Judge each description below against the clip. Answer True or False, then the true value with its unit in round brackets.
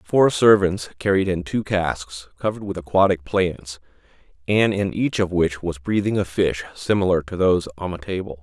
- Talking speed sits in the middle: True (180 wpm)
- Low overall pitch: True (90 Hz)